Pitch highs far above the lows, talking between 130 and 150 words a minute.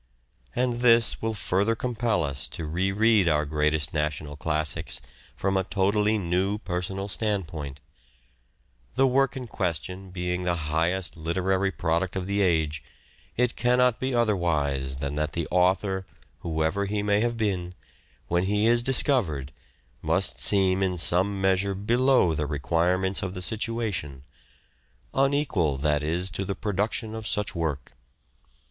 No: average, 4.7 semitones; average, 140 wpm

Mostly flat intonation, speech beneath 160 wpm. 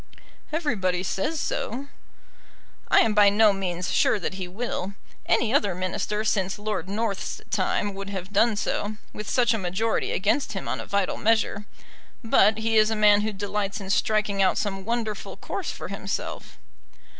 No: narrow, 2.2 semitones; average, 170 wpm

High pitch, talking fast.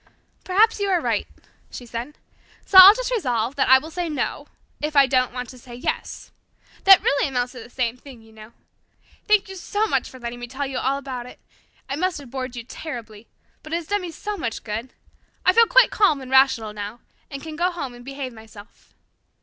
Yes: very high, 270 Hz; fast, 220 wpm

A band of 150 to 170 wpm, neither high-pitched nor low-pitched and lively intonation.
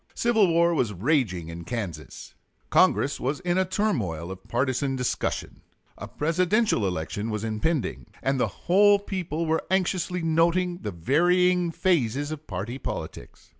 No: average, 140 wpm; medium, 150 Hz; wide, 8.7 semitones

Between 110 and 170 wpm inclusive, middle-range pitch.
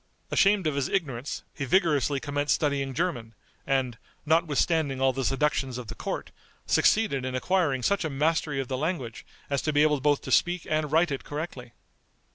No: average, 180 wpm; medium, 145 Hz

